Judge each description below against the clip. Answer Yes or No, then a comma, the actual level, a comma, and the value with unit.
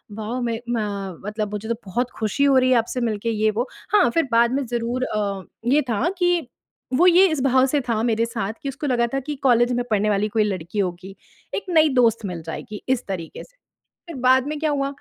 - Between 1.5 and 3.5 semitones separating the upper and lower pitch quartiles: No, average, 4.4 semitones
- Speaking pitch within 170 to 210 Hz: No, high, 235 Hz